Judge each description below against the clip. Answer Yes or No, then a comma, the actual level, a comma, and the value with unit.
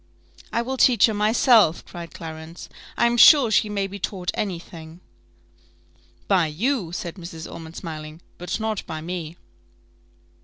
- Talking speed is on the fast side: No, average, 150 wpm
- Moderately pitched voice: Yes, medium, 180 Hz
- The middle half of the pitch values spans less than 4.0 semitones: No, average, 5.0 semitones